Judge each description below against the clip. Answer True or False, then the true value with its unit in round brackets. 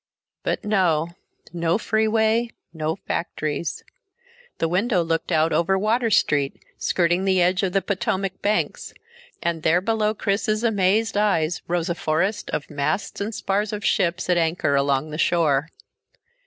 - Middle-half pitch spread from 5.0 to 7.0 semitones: False (4.3 semitones)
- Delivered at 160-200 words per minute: False (145 wpm)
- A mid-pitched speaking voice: True (180 Hz)